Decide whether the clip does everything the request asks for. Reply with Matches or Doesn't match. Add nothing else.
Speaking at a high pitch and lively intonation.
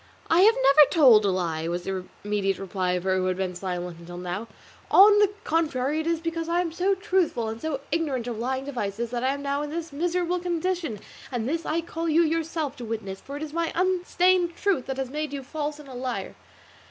Matches